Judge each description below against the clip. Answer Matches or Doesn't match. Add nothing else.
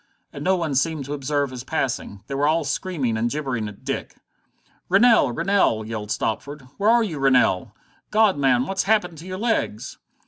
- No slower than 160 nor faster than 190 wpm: Matches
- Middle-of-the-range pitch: Matches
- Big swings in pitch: Matches